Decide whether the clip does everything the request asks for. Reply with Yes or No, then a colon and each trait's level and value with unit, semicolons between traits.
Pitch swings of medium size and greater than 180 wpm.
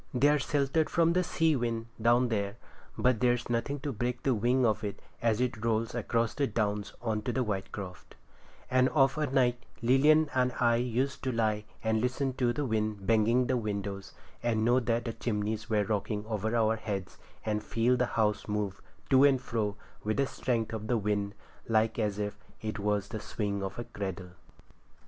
Yes: average, 3.1 semitones; average, 190 wpm